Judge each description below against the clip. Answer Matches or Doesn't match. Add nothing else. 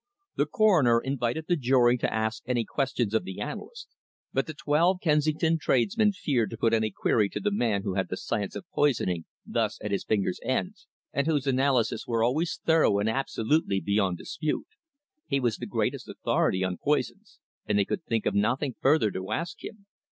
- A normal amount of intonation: Doesn't match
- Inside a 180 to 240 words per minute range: Matches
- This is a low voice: Matches